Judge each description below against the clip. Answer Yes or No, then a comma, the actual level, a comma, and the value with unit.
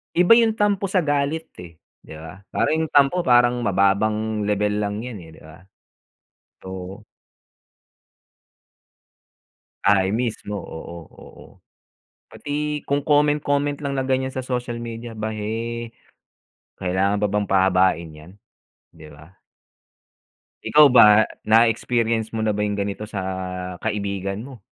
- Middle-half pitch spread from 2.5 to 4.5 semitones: No, average, 5.0 semitones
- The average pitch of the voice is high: No, low, 110 Hz